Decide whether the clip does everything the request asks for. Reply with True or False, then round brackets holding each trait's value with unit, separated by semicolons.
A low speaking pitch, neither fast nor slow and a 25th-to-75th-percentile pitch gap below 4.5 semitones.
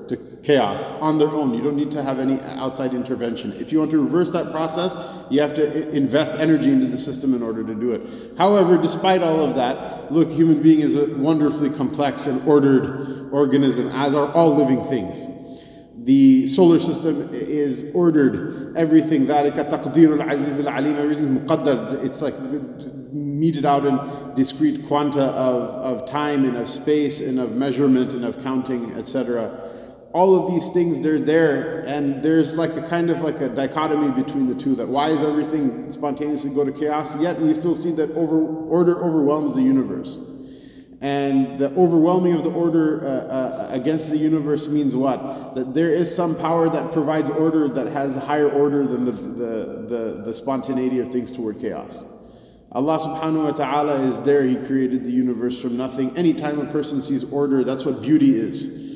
False (145 Hz; 175 wpm; 3.0 semitones)